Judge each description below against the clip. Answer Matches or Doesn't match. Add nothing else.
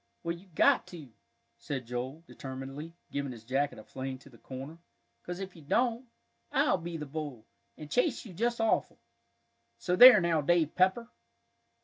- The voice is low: Doesn't match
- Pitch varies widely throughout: Matches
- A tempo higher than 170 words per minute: Doesn't match